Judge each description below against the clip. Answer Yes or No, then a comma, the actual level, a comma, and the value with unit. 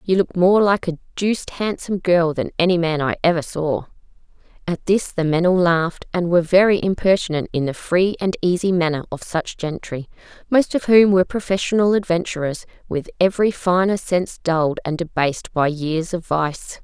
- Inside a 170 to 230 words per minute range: Yes, average, 180 wpm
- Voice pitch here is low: No, medium, 175 Hz